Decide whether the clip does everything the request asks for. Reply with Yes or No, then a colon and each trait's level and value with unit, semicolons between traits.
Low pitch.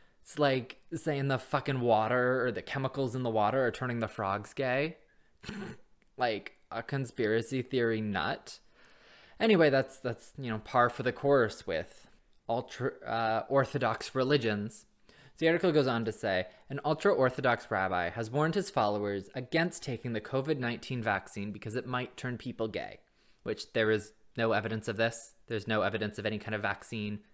Yes: low, 120 Hz